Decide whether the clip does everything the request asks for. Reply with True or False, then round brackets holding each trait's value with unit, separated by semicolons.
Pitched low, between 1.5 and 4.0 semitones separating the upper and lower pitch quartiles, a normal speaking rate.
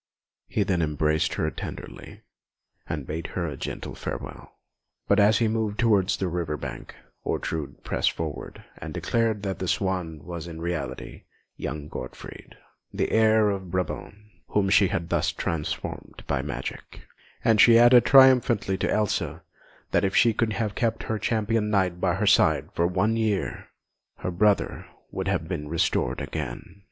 False (95 Hz; 4.6 semitones; 160 wpm)